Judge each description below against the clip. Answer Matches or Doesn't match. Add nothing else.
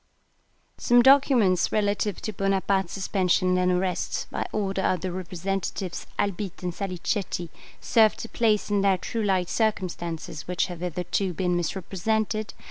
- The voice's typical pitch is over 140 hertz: Matches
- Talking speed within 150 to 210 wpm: Doesn't match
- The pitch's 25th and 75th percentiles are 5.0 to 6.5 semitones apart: Doesn't match